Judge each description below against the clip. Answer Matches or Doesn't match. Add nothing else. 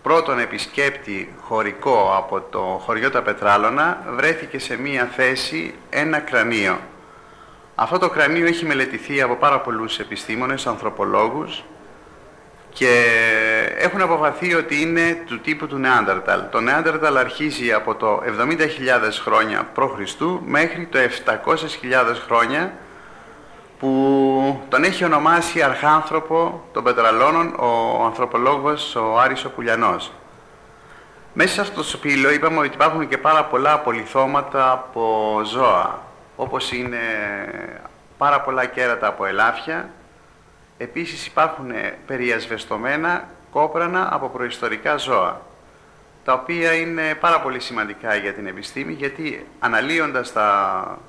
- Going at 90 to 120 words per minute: Matches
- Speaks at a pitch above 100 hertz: Matches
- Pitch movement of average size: Matches